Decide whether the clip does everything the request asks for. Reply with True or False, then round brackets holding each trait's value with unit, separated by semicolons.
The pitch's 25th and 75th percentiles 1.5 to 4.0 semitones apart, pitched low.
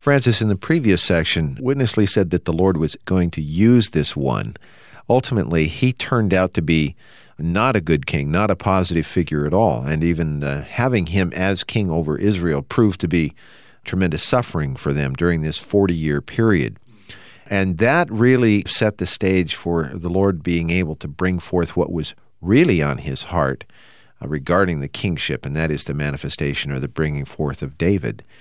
False (4.7 semitones; 90 Hz)